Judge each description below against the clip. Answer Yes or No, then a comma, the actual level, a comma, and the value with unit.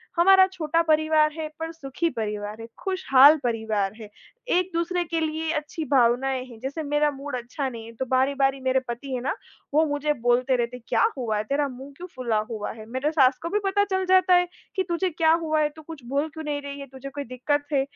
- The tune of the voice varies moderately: Yes, average, 4.1 semitones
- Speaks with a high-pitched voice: Yes, very high, 280 Hz